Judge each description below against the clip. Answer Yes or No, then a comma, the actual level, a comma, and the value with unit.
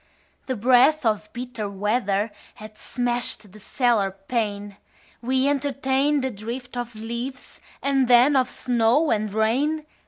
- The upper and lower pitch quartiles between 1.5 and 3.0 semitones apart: No, average, 3.6 semitones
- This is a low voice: No, high, 240 Hz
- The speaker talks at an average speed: No, slow, 130 wpm